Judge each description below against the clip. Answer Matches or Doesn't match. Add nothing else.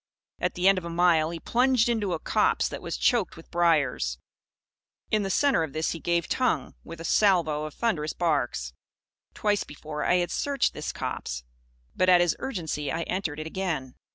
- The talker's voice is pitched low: Doesn't match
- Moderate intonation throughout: Matches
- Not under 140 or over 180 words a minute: Doesn't match